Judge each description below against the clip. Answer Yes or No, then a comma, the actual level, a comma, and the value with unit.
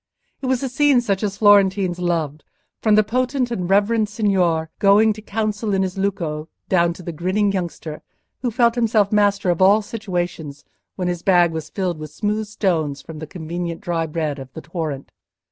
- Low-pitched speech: No, high, 190 Hz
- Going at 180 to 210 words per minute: Yes, average, 185 wpm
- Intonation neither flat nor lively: Yes, average, 4.2 semitones